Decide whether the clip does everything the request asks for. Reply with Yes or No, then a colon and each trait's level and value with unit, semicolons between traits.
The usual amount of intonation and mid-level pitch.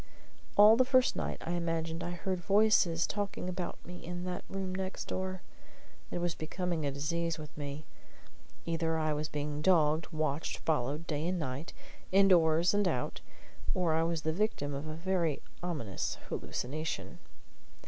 Yes: average, 3.0 semitones; medium, 165 Hz